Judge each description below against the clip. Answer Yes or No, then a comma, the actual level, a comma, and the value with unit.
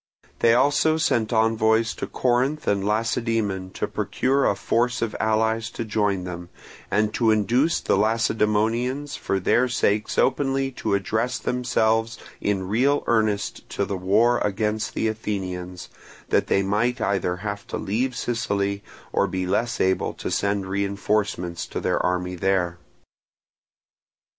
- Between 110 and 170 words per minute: Yes, average, 140 wpm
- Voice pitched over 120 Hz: No, low, 110 Hz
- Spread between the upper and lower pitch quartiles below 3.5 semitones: Yes, average, 3.1 semitones